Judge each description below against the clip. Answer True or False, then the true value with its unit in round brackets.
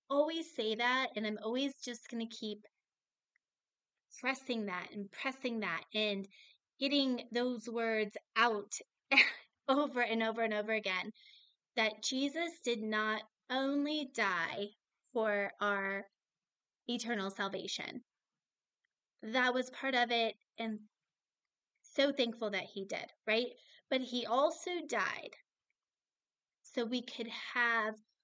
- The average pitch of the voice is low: False (230 Hz)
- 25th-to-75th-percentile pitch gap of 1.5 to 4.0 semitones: True (3.1 semitones)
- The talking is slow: True (120 wpm)